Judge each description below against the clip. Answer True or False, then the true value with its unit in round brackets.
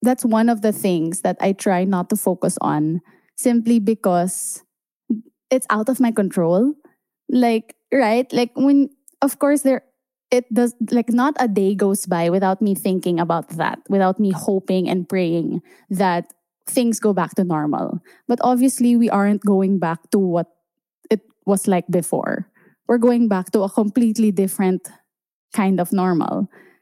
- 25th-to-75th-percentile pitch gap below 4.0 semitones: False (4.6 semitones)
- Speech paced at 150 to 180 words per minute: True (160 wpm)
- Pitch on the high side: True (210 Hz)